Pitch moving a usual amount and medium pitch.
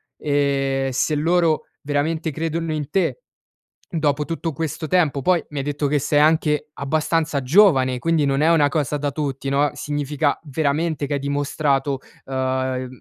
No: narrow, 2.3 semitones; medium, 145 Hz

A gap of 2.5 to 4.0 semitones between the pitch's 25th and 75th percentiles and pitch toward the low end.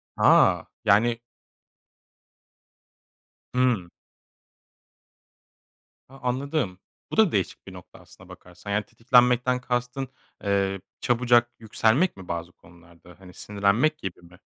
No: average, 4.7 semitones; low, 110 Hz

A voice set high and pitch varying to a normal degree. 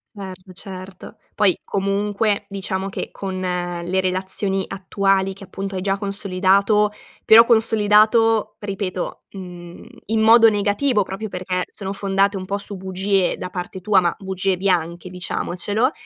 No: high, 195 Hz; narrow, 1.9 semitones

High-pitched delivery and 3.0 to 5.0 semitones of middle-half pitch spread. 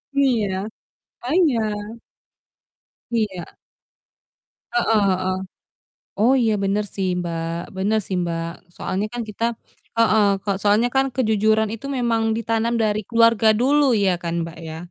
Yes: high, 215 Hz; average, 3.6 semitones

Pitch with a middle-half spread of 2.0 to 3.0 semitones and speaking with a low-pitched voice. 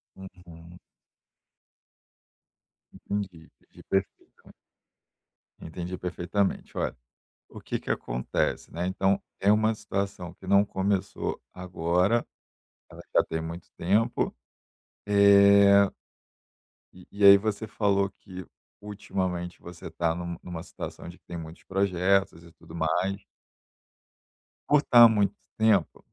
Yes: narrow, 2.6 semitones; very low, 95 Hz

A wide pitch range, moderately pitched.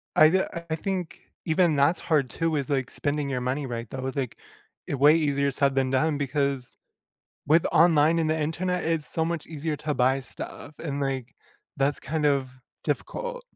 No: average, 2.9 semitones; medium, 145 Hz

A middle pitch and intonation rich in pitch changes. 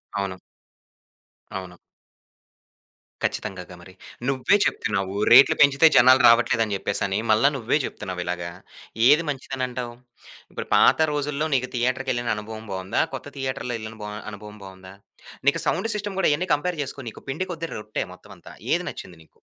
No: low, 120 Hz; wide, 5.9 semitones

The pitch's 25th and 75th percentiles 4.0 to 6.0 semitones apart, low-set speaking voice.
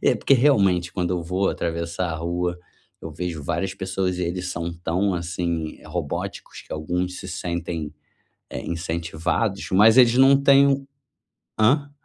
No: average, 2.7 semitones; very low, 90 Hz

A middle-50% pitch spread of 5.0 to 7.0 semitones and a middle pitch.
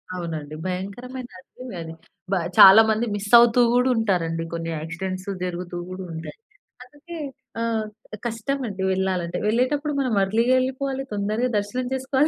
No: wide, 5.5 semitones; high, 215 Hz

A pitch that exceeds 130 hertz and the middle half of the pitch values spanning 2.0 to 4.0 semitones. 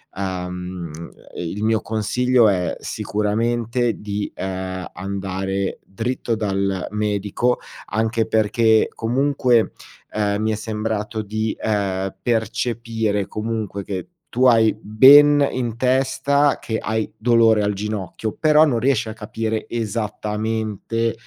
No: low, 110 Hz; narrow, 2.5 semitones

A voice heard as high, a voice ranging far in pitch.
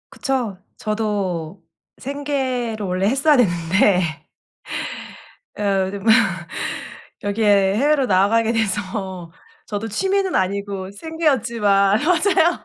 No: high, 210 Hz; average, 4.6 semitones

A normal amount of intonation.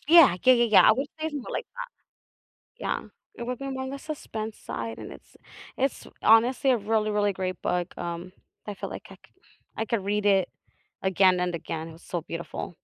No: wide, 5.8 semitones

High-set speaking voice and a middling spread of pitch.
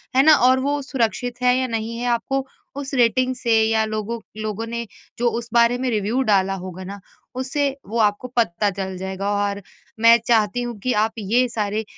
Yes: high, 230 Hz; average, 3.1 semitones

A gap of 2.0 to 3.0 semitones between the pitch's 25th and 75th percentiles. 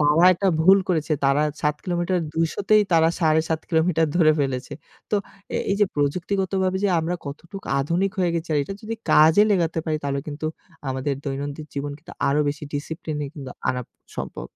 No: average, 3.6 semitones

